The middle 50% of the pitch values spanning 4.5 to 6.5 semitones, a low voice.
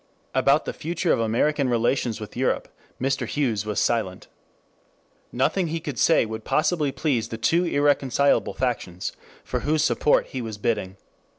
Yes: average, 4.9 semitones; low, 130 Hz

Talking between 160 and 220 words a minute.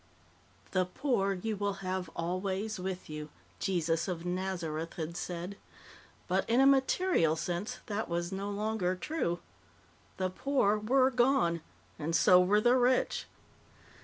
No: slow, 135 wpm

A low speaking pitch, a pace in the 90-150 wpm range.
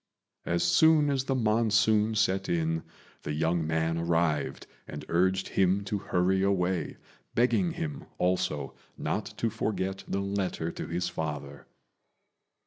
Yes: very low, 95 Hz; slow, 135 wpm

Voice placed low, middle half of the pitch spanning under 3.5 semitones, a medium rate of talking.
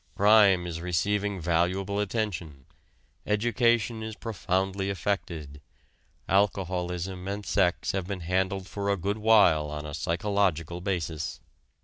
No: very low, 95 Hz; average, 2.9 semitones; slow, 115 wpm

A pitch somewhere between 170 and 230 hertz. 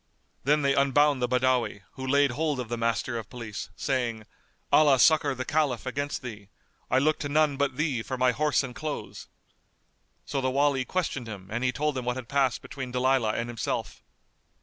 No: low, 130 Hz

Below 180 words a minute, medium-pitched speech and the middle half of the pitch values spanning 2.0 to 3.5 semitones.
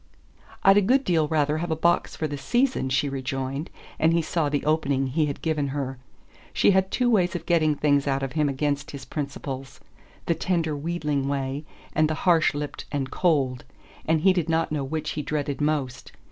No: average, 200 wpm; medium, 150 Hz; average, 2.9 semitones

